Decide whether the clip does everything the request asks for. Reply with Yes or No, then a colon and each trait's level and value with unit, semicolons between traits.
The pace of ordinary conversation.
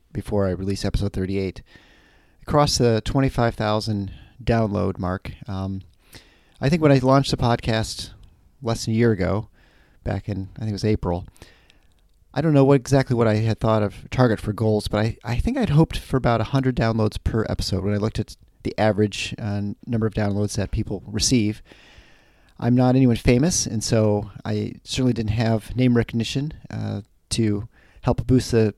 Yes: average, 175 wpm